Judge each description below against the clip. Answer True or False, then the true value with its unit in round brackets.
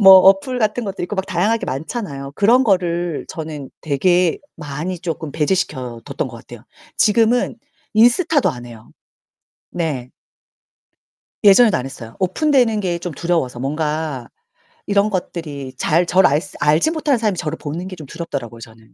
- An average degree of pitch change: False (5.9 semitones)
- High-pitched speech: False (175 Hz)